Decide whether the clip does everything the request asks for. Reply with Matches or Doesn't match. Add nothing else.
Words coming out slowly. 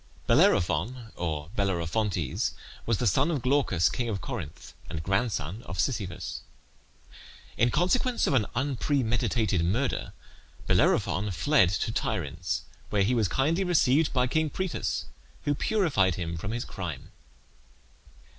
Matches